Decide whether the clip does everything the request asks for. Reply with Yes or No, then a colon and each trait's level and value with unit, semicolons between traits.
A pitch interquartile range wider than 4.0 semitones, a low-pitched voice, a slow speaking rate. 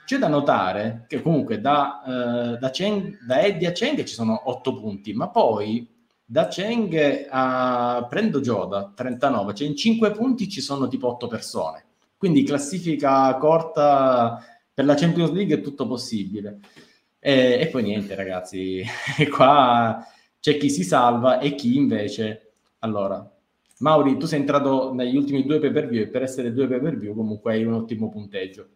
No: average, 4.4 semitones; low, 130 Hz; average, 165 wpm